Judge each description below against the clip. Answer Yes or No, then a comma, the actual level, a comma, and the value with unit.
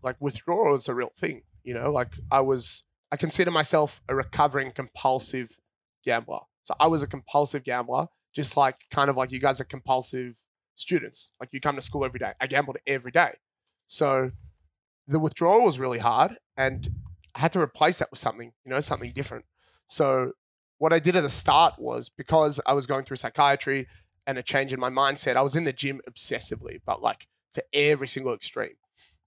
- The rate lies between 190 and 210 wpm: Yes, average, 195 wpm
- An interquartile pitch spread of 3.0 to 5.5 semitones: No, narrow, 2.4 semitones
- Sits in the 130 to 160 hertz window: Yes, low, 135 Hz